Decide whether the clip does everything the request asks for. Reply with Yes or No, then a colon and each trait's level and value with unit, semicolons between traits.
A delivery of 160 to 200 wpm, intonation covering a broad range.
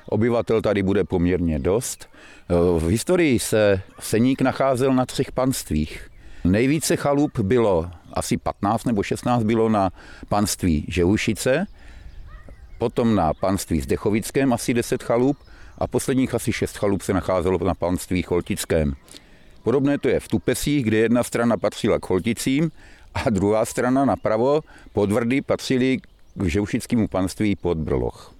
No: average, 135 wpm; wide, 6.1 semitones